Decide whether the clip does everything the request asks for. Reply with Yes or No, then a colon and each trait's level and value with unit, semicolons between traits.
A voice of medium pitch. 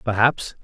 No: low, 115 Hz